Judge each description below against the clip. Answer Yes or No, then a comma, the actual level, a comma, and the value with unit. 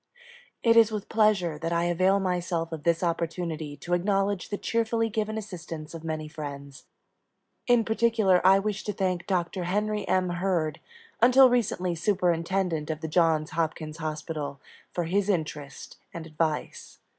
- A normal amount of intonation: Yes, average, 4.0 semitones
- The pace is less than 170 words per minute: Yes, average, 150 wpm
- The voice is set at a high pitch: No, medium, 175 Hz